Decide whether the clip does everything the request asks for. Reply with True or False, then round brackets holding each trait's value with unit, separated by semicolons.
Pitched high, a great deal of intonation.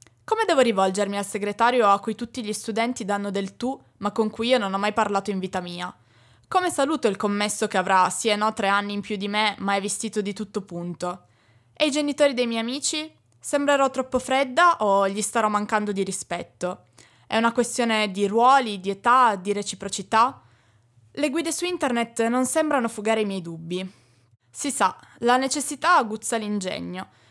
False (215 Hz; 4.1 semitones)